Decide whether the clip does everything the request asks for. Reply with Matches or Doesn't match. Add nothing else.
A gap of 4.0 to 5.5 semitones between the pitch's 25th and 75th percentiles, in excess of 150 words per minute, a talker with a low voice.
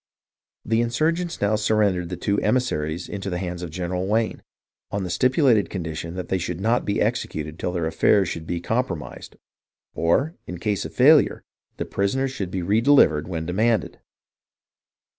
Matches